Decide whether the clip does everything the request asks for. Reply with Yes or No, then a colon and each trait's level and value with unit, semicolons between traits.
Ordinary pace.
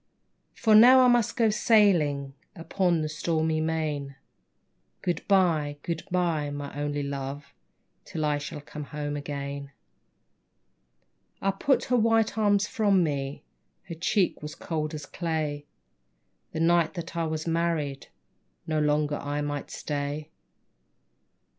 No: slow, 130 wpm